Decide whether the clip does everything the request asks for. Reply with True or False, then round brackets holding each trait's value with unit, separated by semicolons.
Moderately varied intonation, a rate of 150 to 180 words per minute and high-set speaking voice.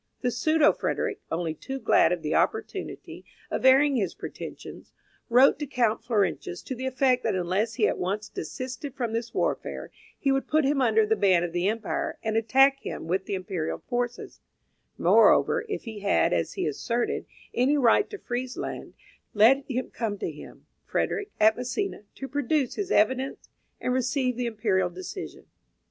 True (4.5 semitones; 170 wpm; 240 Hz)